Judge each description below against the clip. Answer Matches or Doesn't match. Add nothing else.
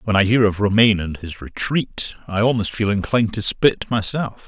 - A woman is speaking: Doesn't match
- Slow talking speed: Doesn't match